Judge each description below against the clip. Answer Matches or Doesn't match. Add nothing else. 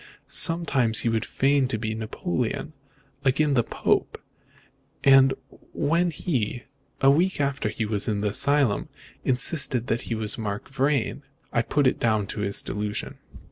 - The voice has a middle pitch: Doesn't match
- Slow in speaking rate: Doesn't match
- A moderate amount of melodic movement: Matches